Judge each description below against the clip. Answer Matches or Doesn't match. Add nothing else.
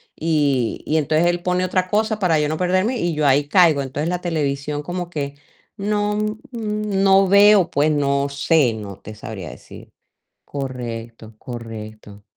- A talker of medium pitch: Matches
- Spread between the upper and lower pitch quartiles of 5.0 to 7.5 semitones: Matches